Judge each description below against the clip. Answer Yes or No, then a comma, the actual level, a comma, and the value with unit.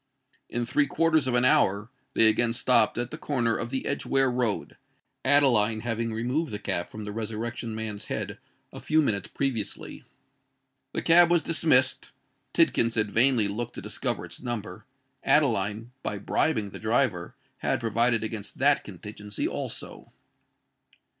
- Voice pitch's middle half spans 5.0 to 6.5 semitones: No, average, 3.7 semitones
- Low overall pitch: Yes, low, 115 Hz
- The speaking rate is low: No, average, 145 wpm